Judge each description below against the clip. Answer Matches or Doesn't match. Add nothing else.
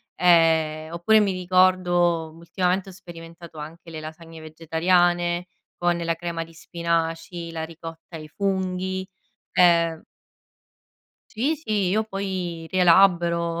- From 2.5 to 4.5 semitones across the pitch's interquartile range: Doesn't match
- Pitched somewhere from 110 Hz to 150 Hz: Doesn't match